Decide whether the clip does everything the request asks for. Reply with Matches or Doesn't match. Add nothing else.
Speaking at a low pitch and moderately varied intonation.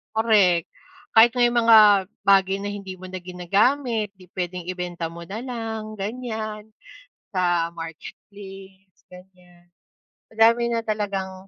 Doesn't match